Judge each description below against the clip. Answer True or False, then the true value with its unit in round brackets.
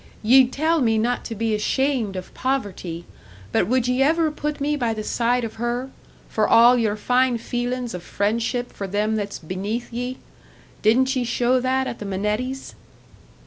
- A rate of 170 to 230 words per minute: True (175 wpm)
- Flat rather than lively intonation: False (3.3 semitones)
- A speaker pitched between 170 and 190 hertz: False (240 Hz)